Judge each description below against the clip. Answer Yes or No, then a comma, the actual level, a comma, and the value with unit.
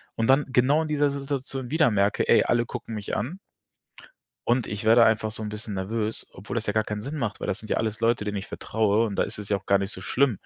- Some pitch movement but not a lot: Yes, average, 3.5 semitones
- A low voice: Yes, low, 110 Hz